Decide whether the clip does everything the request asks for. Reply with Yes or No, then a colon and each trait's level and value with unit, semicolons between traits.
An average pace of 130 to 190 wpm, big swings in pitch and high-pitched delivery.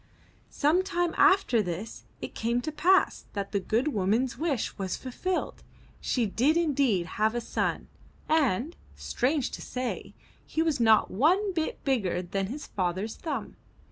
Yes: average, 155 wpm; wide, 7.1 semitones; very high, 250 Hz